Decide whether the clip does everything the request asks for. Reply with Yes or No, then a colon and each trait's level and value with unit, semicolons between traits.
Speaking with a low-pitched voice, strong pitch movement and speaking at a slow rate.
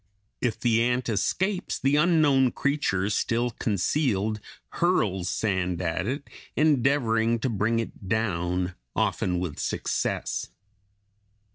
Yes: low, 115 Hz; wide, 6.1 semitones; slow, 110 wpm